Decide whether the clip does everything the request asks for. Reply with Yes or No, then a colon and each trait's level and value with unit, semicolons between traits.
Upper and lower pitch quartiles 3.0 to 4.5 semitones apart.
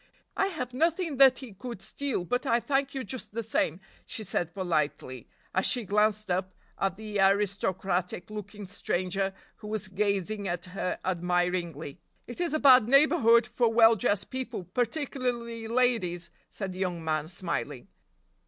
No: average, 5.1 semitones